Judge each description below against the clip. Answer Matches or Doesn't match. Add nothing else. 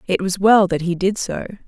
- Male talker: Doesn't match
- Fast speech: Matches